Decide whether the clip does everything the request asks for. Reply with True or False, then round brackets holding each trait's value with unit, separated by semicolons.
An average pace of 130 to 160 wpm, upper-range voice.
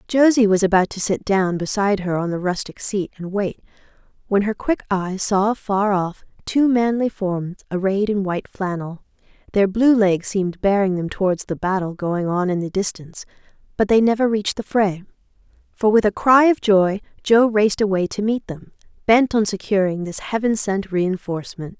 False (185 wpm; 200 Hz)